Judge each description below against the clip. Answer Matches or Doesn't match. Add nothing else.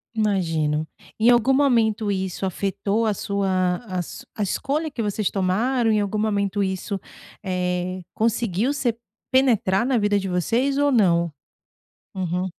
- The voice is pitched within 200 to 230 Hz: Matches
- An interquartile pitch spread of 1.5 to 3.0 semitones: Doesn't match